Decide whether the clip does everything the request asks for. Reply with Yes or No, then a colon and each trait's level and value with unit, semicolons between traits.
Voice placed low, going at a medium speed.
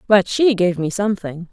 No: high, 190 Hz; average, 195 wpm